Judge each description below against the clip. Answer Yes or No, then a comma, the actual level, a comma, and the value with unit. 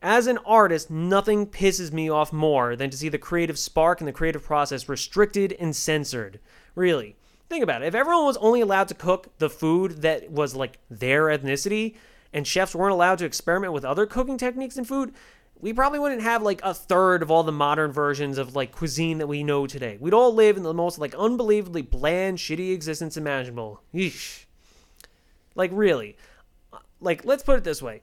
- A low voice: No, medium, 170 Hz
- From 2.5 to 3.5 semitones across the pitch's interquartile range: No, wide, 5.6 semitones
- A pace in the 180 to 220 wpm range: Yes, average, 195 wpm